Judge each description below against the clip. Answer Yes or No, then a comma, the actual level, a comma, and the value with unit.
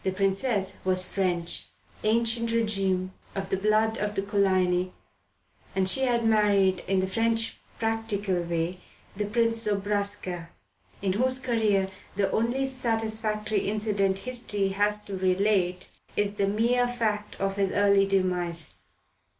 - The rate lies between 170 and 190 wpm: No, slow, 135 wpm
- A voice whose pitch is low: No, high, 205 Hz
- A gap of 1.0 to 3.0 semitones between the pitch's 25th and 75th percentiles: Yes, average, 2.7 semitones